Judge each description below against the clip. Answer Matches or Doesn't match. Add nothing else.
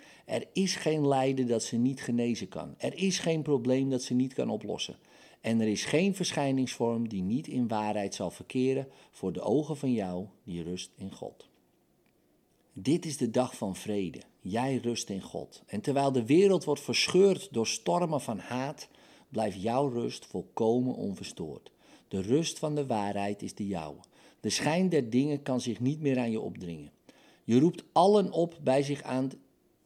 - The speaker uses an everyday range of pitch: Matches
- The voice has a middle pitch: Doesn't match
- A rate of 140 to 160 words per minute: Doesn't match